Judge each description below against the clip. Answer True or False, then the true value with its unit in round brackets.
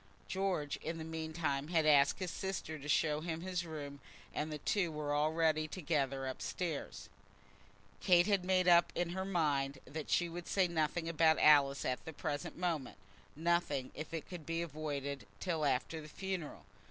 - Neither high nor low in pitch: True (160 Hz)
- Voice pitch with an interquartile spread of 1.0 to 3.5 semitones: True (2.9 semitones)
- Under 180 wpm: True (170 wpm)